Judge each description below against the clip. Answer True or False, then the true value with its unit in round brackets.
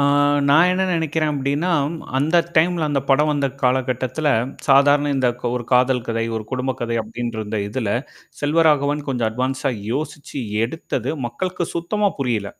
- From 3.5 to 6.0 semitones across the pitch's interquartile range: True (3.8 semitones)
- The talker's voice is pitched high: False (135 Hz)